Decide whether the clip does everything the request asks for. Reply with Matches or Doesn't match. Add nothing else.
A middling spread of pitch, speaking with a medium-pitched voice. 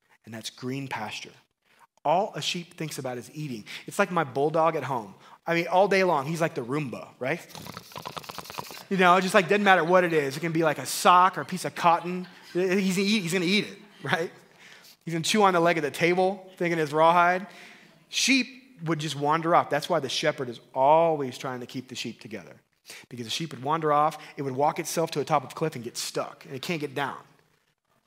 Matches